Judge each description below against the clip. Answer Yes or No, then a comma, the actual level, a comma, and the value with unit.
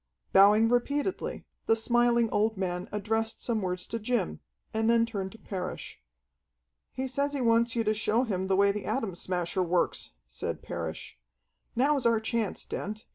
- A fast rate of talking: No, average, 165 wpm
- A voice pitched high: Yes, high, 220 Hz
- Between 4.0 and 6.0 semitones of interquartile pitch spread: No, average, 3.6 semitones